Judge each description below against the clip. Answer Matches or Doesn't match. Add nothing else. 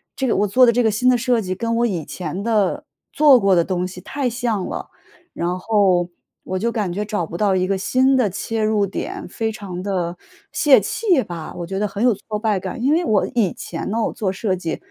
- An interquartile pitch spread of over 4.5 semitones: Doesn't match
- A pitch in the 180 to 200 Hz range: Doesn't match